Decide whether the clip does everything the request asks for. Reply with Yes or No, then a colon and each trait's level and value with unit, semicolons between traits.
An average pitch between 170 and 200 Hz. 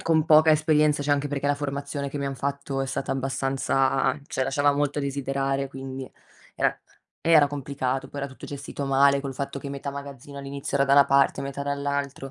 No: medium, 140 Hz